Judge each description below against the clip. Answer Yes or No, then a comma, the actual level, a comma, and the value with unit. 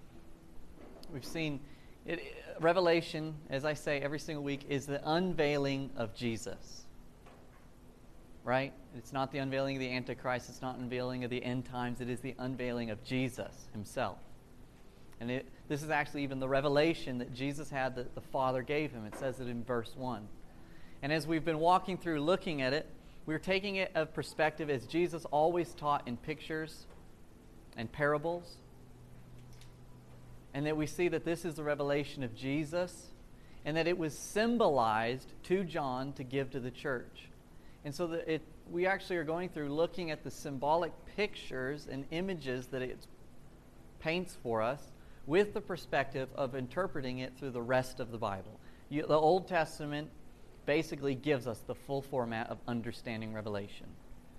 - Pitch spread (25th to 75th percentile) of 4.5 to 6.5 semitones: No, average, 4.1 semitones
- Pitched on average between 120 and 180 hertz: Yes, medium, 140 Hz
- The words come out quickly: No, average, 165 wpm